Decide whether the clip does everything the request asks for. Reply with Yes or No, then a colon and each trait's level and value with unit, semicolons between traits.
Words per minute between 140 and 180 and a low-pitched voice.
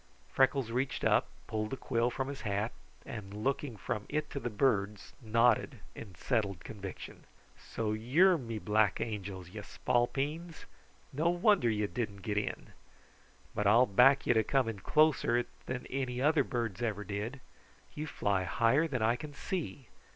Yes: average, 160 wpm; low, 115 Hz